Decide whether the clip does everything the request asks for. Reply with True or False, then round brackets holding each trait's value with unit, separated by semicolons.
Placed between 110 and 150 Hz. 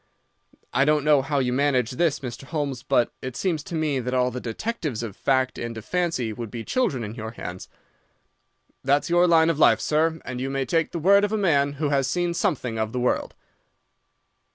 True (140 Hz)